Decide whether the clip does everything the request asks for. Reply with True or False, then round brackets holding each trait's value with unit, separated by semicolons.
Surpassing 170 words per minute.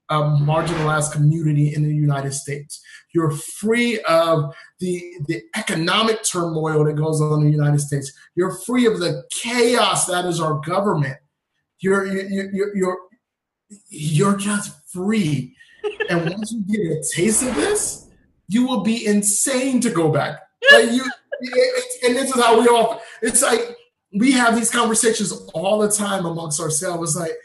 False (165 wpm)